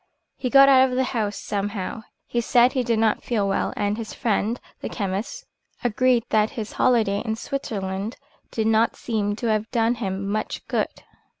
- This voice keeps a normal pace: Yes, average, 180 wpm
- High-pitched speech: Yes, high, 225 Hz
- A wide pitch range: No, average, 3.0 semitones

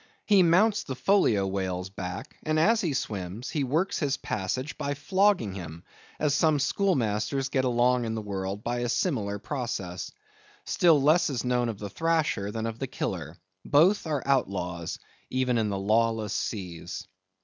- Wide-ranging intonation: Yes, wide, 7.0 semitones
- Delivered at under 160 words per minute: No, average, 165 wpm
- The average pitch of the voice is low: Yes, low, 120 Hz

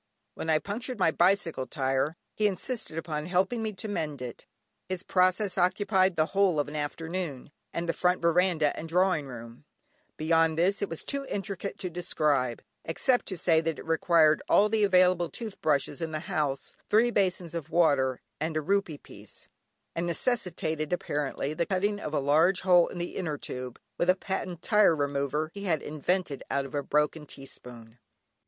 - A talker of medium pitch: Yes, medium, 170 Hz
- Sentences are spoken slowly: No, average, 180 wpm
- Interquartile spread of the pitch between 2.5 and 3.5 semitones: No, average, 4.0 semitones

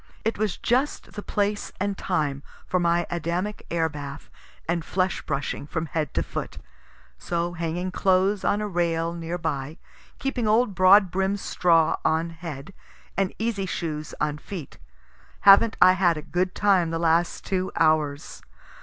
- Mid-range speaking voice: Yes, medium, 175 Hz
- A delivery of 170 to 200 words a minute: No, average, 155 wpm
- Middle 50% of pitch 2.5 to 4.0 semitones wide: Yes, average, 3.2 semitones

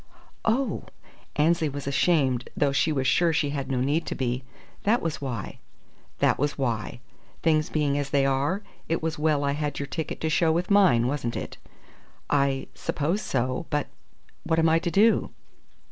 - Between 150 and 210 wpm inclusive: Yes, average, 175 wpm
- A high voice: No, medium, 145 Hz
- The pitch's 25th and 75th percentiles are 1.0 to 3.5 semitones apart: Yes, average, 3.2 semitones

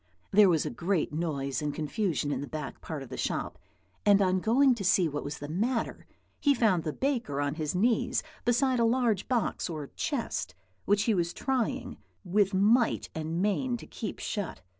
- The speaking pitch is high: Yes, high, 195 Hz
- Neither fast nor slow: Yes, average, 190 wpm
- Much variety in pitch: Yes, wide, 7.0 semitones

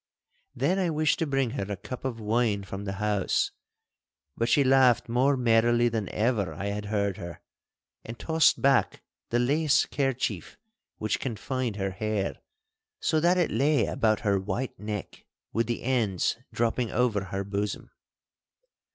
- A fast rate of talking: No, average, 155 wpm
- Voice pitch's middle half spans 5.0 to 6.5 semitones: No, average, 4.5 semitones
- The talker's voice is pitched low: Yes, low, 115 Hz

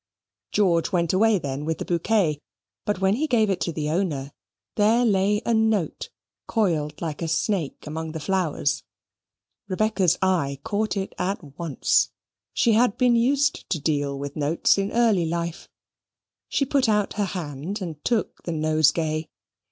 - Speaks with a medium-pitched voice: Yes, medium, 180 Hz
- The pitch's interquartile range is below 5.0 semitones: No, average, 5.3 semitones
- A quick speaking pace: No, average, 160 wpm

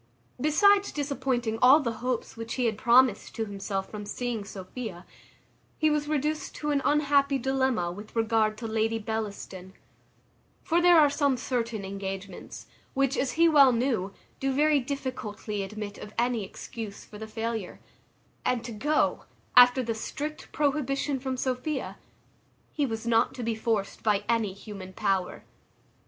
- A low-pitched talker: No, high, 235 Hz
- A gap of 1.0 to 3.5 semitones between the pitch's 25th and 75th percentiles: No, average, 4.4 semitones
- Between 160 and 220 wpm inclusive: No, average, 150 wpm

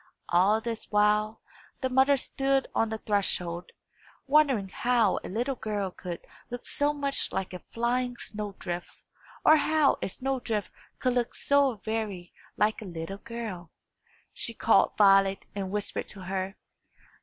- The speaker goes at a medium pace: Yes, average, 150 wpm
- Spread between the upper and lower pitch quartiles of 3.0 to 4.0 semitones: No, average, 4.4 semitones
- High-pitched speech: Yes, high, 215 Hz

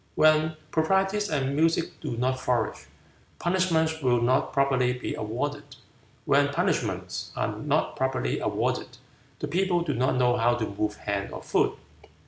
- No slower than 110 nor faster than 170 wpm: Yes, average, 145 wpm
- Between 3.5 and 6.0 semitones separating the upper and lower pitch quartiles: Yes, average, 4.4 semitones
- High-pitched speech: No, low, 135 Hz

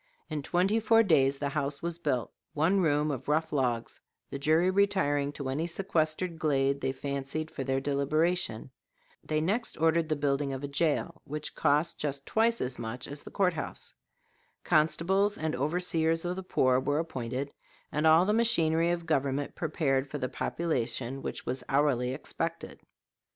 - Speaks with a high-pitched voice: No, medium, 150 Hz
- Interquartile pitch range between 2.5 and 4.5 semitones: Yes, average, 3.5 semitones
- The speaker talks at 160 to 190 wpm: Yes, average, 170 wpm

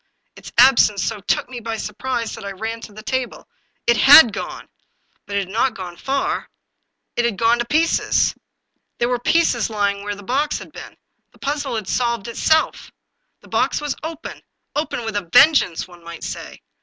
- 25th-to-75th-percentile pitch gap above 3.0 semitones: Yes, average, 4.5 semitones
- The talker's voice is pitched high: Yes, high, 235 Hz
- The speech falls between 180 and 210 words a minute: Yes, average, 190 wpm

